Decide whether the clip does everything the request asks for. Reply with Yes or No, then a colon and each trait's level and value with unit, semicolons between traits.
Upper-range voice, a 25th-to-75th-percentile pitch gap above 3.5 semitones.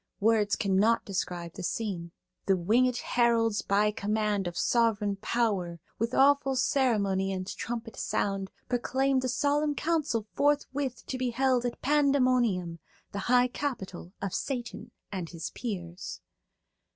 Yes: high, 225 Hz; average, 4.7 semitones